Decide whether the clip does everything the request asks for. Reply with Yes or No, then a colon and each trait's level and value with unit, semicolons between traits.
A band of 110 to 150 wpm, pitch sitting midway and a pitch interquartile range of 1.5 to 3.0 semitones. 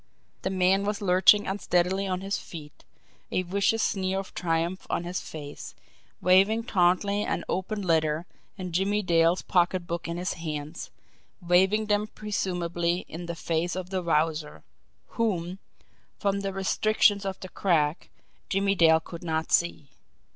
Yes: average, 145 wpm; medium, 180 Hz; narrow, 2.6 semitones